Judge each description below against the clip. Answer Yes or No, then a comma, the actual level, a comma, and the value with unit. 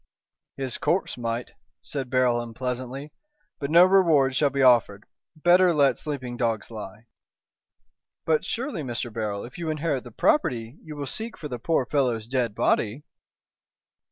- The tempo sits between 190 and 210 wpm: No, average, 150 wpm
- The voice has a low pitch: Yes, low, 130 Hz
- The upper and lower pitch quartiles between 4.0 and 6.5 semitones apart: Yes, average, 4.3 semitones